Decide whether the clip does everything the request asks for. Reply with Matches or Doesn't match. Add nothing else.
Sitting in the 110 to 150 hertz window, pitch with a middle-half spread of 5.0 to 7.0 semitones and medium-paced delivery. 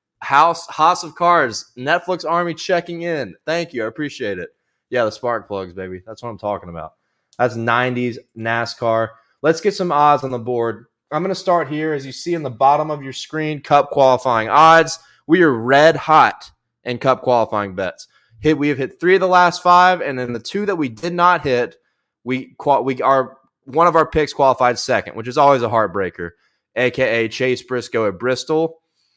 Matches